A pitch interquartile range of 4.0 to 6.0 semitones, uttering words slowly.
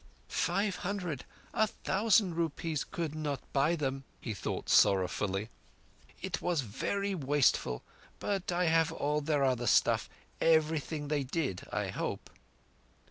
Yes: average, 4.3 semitones; slow, 115 wpm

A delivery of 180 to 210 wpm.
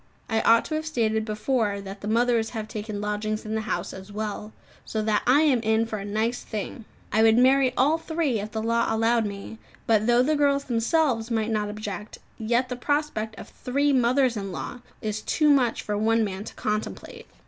Yes: fast, 205 wpm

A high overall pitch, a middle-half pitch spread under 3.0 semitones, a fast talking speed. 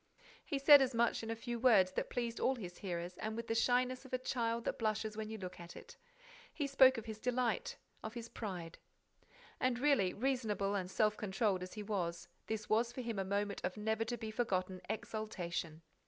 No: high, 220 Hz; average, 3.8 semitones; fast, 210 wpm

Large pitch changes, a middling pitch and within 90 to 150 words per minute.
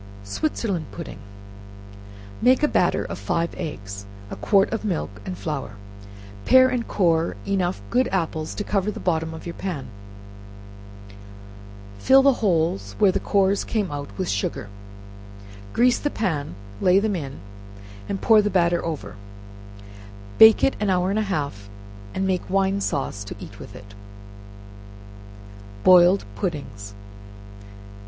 Yes: wide, 6.1 semitones; medium, 180 Hz; average, 140 wpm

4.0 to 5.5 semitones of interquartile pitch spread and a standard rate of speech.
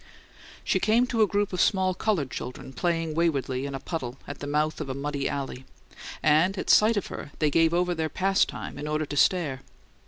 No: average, 4.7 semitones; fast, 210 wpm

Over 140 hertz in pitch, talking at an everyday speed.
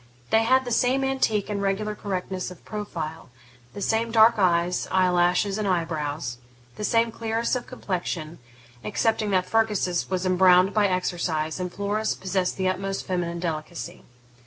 Yes: high, 190 Hz; average, 160 wpm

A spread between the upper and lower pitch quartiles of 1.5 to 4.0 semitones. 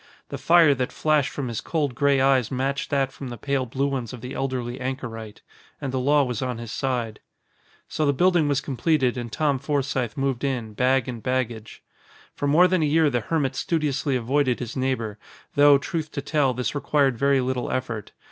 Yes: narrow, 2.6 semitones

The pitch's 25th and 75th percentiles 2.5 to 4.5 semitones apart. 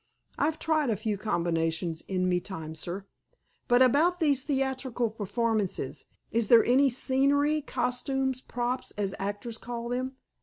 No: average, 5.2 semitones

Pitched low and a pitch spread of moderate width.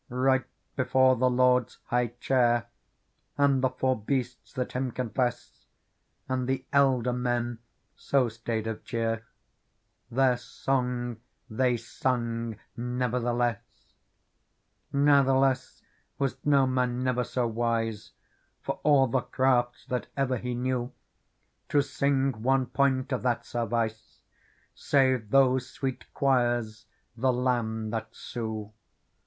No: low, 125 Hz; narrow, 1.9 semitones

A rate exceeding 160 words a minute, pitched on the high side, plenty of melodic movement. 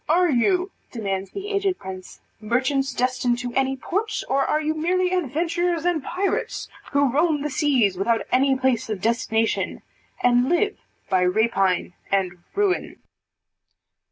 No: average, 140 wpm; very high, 270 Hz; wide, 7.4 semitones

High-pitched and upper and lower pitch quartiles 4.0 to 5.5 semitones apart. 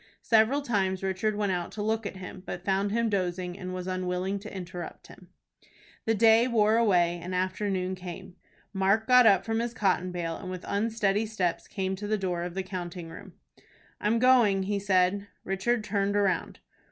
No: high, 195 Hz; average, 2.8 semitones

